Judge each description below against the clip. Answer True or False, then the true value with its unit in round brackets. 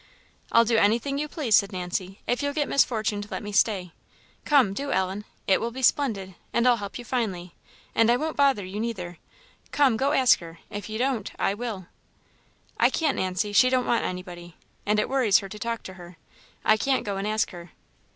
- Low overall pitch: False (215 Hz)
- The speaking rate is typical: False (210 wpm)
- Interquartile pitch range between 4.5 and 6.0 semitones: True (4.9 semitones)